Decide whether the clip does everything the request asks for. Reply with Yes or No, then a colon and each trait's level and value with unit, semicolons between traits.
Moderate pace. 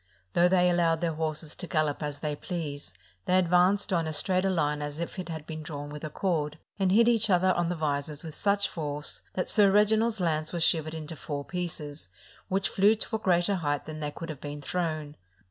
No: fast, 220 wpm